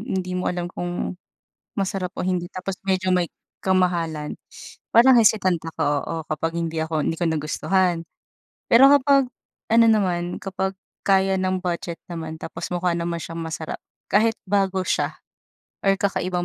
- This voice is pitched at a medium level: Yes, medium, 180 Hz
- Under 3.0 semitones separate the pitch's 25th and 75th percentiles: Yes, narrow, 2.5 semitones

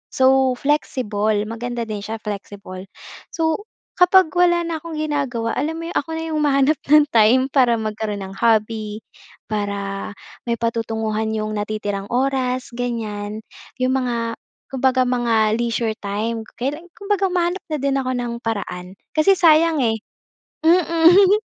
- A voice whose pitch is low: No, high, 245 Hz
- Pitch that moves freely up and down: Yes, wide, 6.0 semitones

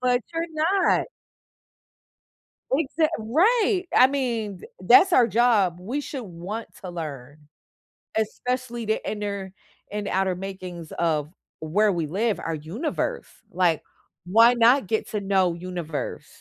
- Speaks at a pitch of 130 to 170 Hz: No, high, 210 Hz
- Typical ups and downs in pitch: No, wide, 6.0 semitones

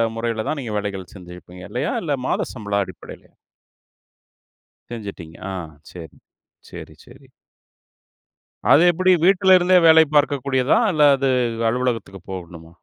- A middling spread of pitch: No, wide, 7.8 semitones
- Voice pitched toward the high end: No, low, 115 Hz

